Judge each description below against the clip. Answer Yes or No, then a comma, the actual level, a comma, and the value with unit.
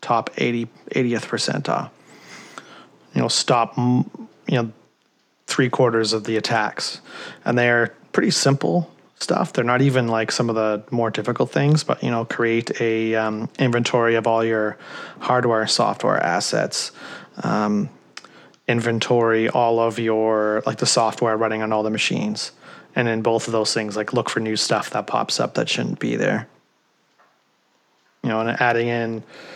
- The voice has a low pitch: Yes, low, 115 Hz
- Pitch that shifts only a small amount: Yes, narrow, 1.9 semitones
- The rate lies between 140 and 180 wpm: Yes, average, 160 wpm